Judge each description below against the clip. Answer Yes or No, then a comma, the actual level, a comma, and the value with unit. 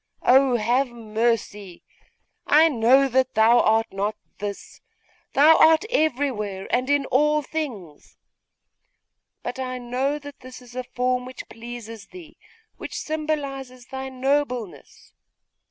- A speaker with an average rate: No, slow, 120 wpm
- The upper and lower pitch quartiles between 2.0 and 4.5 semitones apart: Yes, average, 3.6 semitones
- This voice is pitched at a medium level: No, very high, 255 Hz